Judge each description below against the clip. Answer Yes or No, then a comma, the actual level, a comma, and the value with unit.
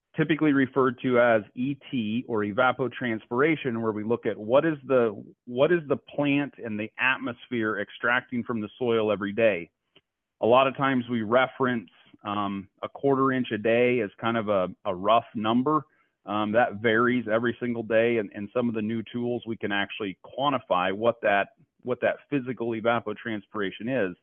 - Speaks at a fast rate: No, average, 175 wpm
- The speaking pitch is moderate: No, low, 120 Hz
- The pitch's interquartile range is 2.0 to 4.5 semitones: Yes, average, 3.0 semitones